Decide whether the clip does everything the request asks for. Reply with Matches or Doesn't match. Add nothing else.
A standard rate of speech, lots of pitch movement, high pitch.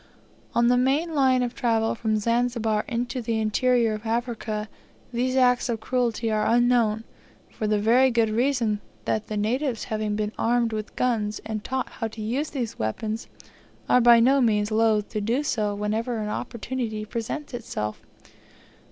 Doesn't match